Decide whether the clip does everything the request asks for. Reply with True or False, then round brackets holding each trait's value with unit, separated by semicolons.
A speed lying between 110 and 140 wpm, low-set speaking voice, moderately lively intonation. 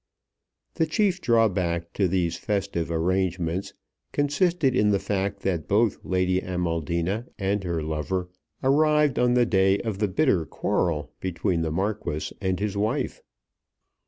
True (135 wpm; 95 Hz; 4.5 semitones)